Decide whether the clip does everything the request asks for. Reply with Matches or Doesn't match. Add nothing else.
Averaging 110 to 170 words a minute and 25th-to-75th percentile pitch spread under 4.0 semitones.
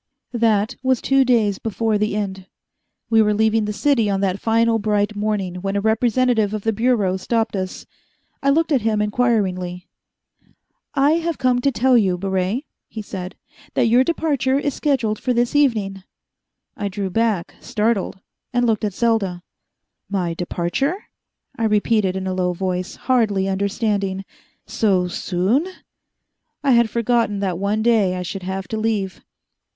Matches